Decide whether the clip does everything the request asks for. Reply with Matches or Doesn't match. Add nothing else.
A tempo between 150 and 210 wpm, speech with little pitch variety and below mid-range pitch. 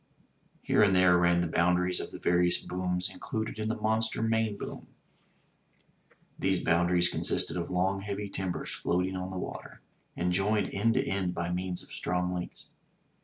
Matches